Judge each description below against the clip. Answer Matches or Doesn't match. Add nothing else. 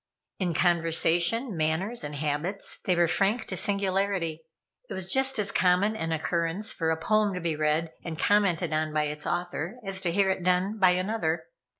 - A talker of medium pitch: Matches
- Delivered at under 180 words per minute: Doesn't match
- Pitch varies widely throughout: Doesn't match